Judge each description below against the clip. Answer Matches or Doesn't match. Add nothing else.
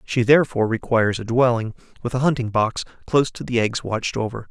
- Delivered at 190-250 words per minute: Matches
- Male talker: Matches